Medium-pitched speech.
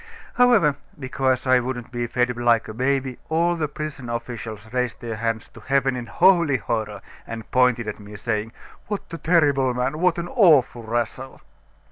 No: low, 125 Hz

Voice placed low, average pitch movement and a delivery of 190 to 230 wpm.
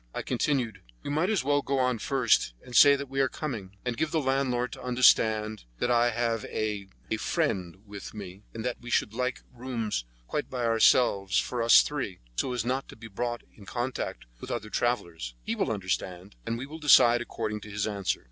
Yes: low, 120 Hz; average, 3.7 semitones; fast, 205 wpm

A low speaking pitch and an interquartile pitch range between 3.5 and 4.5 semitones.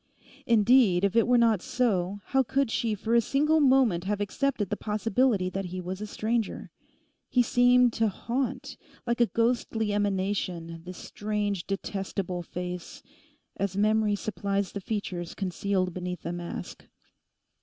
No: high, 205 Hz; average, 3.9 semitones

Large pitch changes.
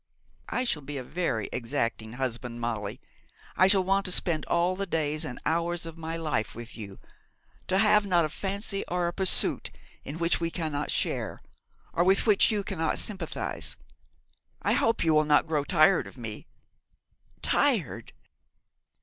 Yes: wide, 5.7 semitones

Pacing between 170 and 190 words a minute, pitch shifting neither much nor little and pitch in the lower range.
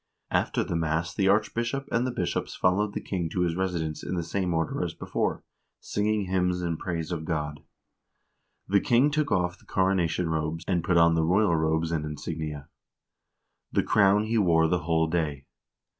Yes: average, 180 wpm; average, 3.2 semitones; very low, 85 Hz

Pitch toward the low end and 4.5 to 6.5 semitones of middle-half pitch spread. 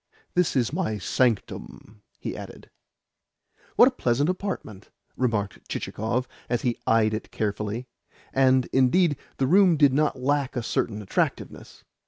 Yes: low, 125 Hz; average, 4.9 semitones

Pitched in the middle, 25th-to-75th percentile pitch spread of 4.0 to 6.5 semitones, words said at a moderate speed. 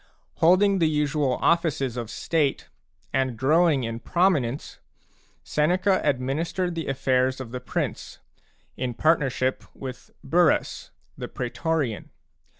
No: medium, 145 Hz; average, 4.4 semitones; slow, 110 wpm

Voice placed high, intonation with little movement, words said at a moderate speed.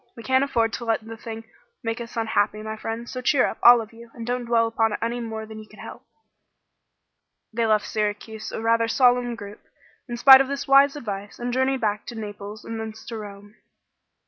No: high, 225 Hz; narrow, 1.8 semitones; fast, 215 wpm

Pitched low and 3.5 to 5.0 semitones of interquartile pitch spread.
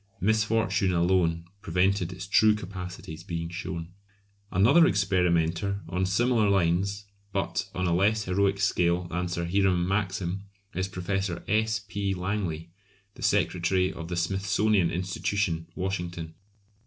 No: very low, 95 Hz; narrow, 2.4 semitones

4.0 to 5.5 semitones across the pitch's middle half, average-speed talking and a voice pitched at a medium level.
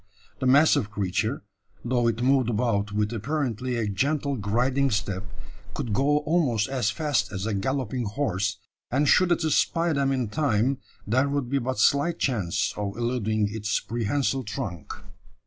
No: average, 4.9 semitones; average, 155 wpm; low, 120 Hz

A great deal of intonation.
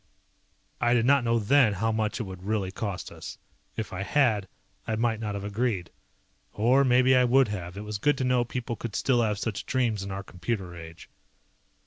No: average, 3.6 semitones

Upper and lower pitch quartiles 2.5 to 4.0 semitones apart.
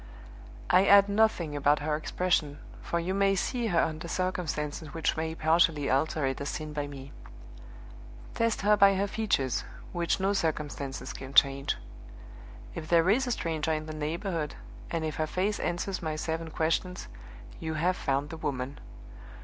Yes: average, 3.7 semitones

